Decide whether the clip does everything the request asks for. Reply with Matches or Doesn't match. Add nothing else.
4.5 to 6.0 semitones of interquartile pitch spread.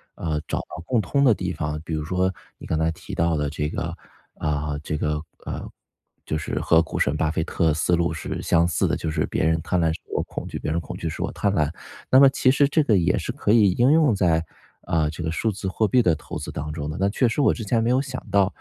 Matches